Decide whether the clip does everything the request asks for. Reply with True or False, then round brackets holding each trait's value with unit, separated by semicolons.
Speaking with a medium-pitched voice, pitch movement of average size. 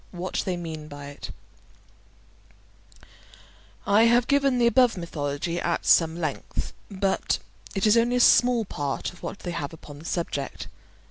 False (175 Hz; 6.7 semitones)